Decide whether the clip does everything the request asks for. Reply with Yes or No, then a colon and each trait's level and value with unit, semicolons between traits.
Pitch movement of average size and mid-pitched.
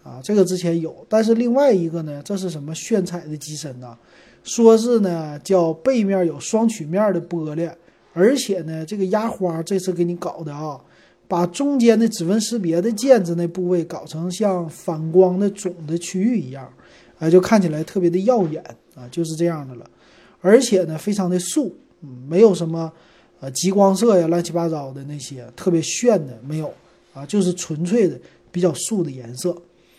Yes: average, 4.0 semitones; medium, 175 Hz